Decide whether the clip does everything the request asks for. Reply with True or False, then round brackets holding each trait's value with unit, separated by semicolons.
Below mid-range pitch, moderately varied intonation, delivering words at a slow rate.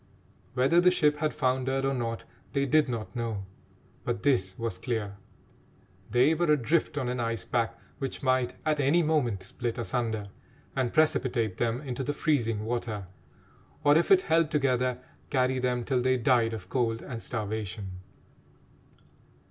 False (125 Hz; 3.6 semitones; 155 wpm)